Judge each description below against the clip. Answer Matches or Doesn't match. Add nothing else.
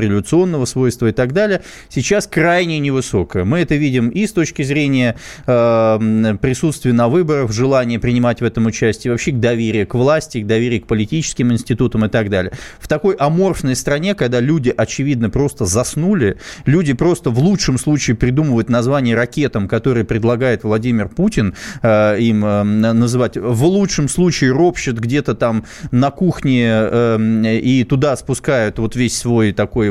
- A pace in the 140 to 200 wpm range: Matches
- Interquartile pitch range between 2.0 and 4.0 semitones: Doesn't match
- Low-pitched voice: Matches